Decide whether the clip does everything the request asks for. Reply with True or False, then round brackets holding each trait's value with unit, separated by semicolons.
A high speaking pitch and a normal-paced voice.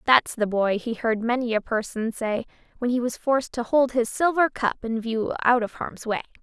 False (235 Hz; 225 wpm)